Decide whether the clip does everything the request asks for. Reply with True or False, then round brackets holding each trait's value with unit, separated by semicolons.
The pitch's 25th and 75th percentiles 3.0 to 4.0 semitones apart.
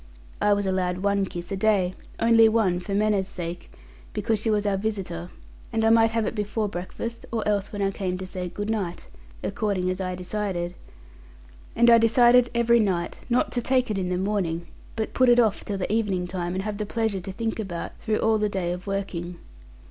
True (3.4 semitones)